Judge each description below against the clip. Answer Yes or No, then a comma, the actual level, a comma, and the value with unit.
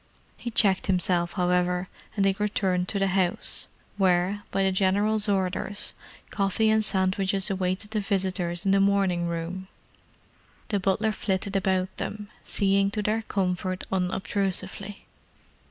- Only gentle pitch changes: Yes, narrow, 1.6 semitones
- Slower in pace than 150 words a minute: Yes, slow, 135 wpm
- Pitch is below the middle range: No, high, 195 Hz